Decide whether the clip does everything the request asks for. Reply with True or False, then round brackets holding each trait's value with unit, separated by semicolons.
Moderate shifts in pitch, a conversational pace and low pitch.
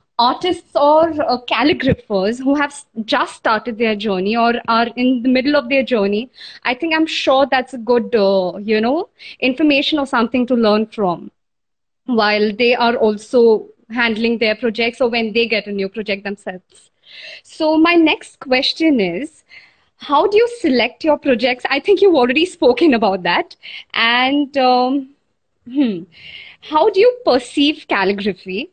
False (4.6 semitones; 155 wpm; 250 Hz)